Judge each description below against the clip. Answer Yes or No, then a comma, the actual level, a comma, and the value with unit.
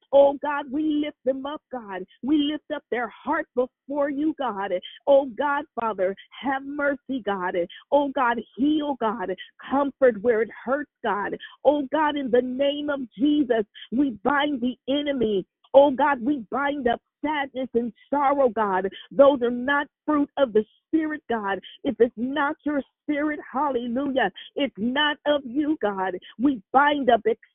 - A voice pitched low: No, very high, 275 Hz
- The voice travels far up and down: No, average, 3.5 semitones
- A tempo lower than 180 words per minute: Yes, average, 155 wpm